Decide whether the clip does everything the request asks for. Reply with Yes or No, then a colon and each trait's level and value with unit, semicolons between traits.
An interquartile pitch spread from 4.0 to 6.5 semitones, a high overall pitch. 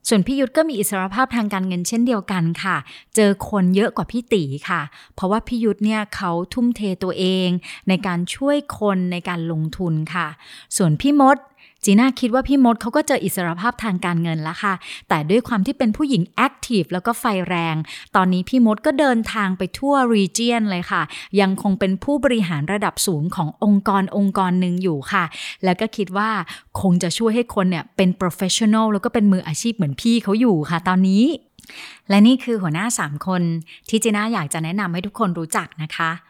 Yes: average, 4.4 semitones; high, 200 Hz